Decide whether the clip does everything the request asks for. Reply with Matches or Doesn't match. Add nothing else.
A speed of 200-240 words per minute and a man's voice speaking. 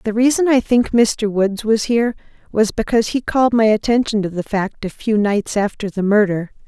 Doesn't match